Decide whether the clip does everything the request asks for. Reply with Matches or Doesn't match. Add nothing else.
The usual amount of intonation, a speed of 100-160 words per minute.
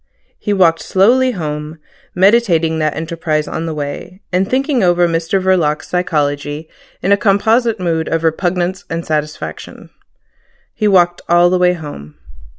Matches